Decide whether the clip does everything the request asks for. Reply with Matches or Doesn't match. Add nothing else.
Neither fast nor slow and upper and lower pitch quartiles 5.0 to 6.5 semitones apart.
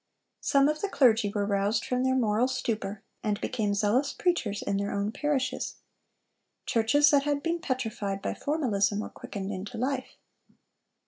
Matches